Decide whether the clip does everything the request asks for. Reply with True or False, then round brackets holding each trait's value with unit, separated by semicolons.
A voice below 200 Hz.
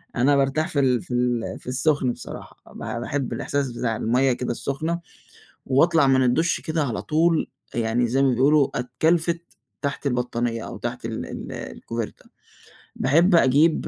True (135 Hz)